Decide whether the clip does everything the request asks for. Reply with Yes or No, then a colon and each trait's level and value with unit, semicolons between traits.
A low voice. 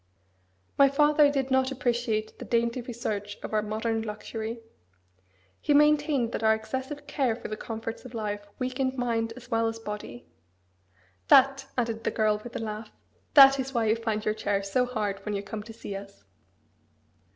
No: high, 230 Hz